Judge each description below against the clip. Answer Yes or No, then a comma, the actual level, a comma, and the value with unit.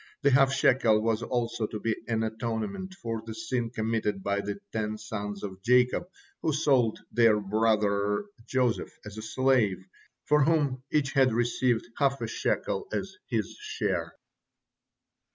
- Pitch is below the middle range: Yes, low, 115 Hz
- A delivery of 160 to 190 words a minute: No, average, 150 wpm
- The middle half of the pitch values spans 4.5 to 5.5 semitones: No, average, 3.6 semitones